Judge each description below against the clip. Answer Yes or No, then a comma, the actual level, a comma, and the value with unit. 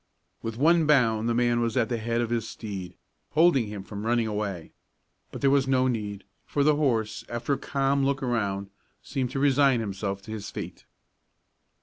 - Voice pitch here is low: Yes, low, 120 Hz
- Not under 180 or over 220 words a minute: Yes, average, 190 wpm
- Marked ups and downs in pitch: No, average, 4.1 semitones